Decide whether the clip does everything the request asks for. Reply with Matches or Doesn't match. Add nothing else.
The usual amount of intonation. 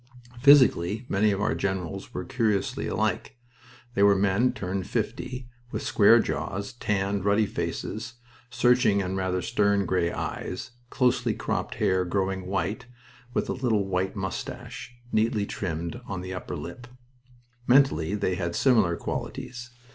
Matches